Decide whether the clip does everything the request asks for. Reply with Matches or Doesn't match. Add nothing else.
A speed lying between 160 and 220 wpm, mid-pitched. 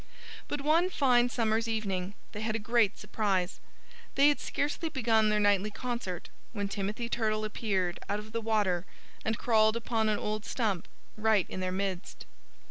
Doesn't match